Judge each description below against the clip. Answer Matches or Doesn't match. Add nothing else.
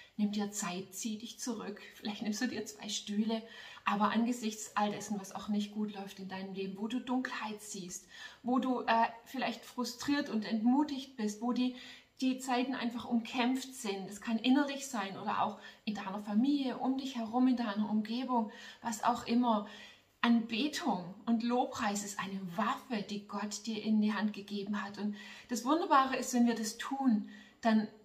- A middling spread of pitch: Matches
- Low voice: Doesn't match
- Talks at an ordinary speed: Matches